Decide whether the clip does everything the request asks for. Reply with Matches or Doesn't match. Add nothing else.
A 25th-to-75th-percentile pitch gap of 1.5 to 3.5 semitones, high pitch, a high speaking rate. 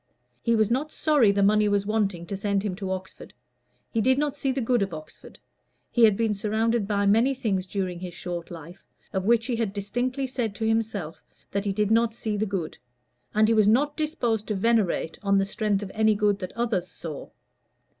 Matches